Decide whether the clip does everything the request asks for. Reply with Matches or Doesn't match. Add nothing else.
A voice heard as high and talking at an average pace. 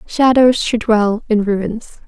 Matches